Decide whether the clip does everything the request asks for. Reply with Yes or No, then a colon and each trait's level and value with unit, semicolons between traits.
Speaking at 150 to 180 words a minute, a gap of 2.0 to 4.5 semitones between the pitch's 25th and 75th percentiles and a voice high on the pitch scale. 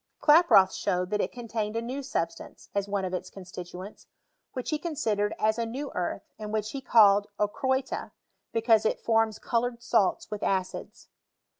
Yes: average, 165 wpm; average, 3.3 semitones; high, 215 Hz